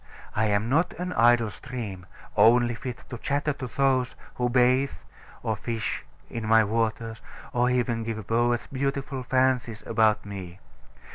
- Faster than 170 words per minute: No, average, 150 wpm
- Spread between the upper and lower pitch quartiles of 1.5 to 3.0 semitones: Yes, narrow, 2.5 semitones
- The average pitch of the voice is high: No, low, 120 Hz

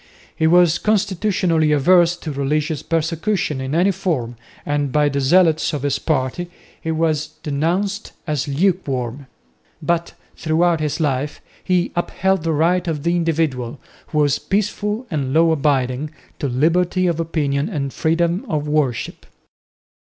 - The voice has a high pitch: No, medium, 160 Hz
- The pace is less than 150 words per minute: Yes, average, 140 wpm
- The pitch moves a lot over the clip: No, average, 3.3 semitones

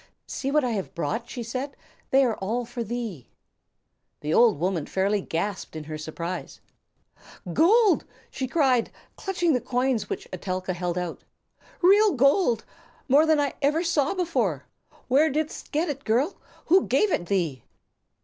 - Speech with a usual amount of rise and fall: No, wide, 8.0 semitones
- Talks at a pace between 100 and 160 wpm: Yes, average, 155 wpm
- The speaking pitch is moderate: No, high, 245 Hz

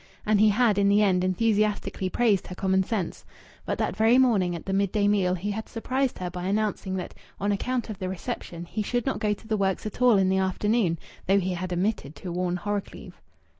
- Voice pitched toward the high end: Yes, high, 200 Hz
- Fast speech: Yes, fast, 220 wpm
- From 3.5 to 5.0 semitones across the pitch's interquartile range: No, narrow, 2.6 semitones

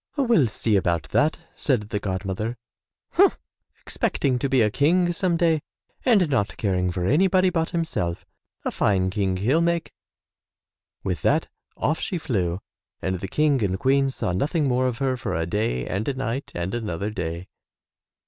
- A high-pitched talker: No, low, 120 Hz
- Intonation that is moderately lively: No, wide, 8.3 semitones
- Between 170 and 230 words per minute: Yes, average, 175 wpm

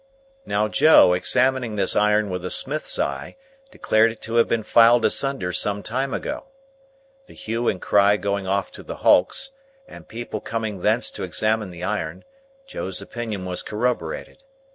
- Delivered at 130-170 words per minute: Yes, average, 165 wpm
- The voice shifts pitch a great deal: No, average, 3.6 semitones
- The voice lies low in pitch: Yes, low, 105 Hz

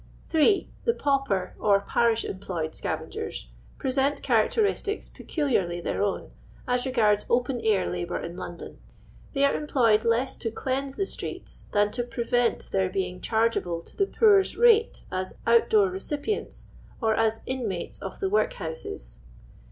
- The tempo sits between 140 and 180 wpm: Yes, average, 150 wpm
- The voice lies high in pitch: Yes, high, 230 Hz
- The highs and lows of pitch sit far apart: Yes, wide, 6.1 semitones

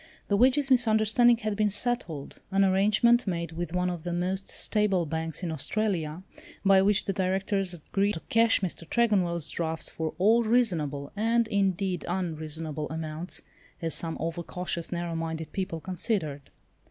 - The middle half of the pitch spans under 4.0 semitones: No, average, 4.4 semitones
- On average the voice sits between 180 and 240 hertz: Yes, medium, 185 Hz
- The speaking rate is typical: Yes, average, 155 wpm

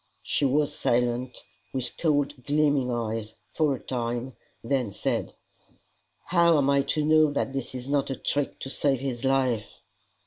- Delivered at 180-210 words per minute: No, average, 160 wpm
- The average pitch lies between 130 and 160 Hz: Yes, low, 135 Hz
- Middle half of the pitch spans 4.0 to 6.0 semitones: No, average, 2.8 semitones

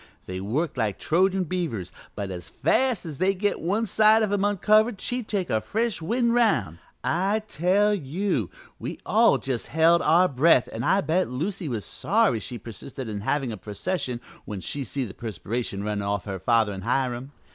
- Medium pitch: Yes, medium, 150 Hz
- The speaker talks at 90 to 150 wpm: No, average, 185 wpm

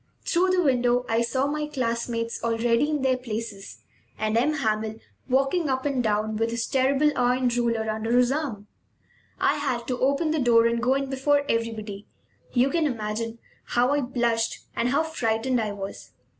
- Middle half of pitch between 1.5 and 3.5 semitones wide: Yes, average, 3.1 semitones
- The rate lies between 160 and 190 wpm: Yes, average, 175 wpm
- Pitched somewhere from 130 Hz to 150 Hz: No, high, 245 Hz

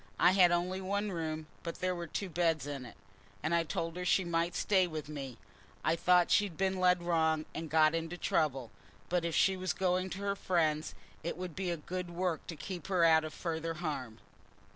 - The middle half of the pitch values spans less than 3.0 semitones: Yes, narrow, 2.5 semitones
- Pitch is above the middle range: No, medium, 170 Hz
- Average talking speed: No, fast, 210 wpm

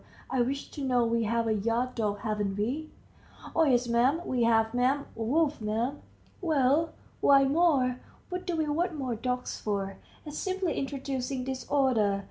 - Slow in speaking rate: No, average, 160 wpm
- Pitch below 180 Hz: No, very high, 255 Hz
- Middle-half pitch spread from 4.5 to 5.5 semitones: No, average, 4.0 semitones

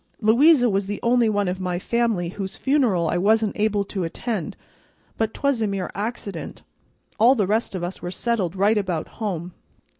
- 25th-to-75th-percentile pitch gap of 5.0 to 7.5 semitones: No, average, 3.8 semitones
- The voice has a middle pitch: No, high, 205 Hz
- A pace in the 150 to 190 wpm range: Yes, average, 180 wpm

